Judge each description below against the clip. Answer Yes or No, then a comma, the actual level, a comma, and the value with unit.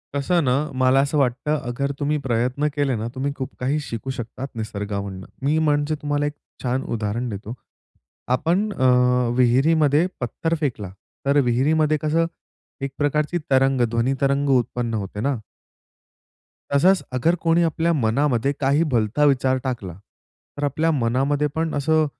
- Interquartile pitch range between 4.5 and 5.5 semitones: No, average, 3.7 semitones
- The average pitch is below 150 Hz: Yes, medium, 140 Hz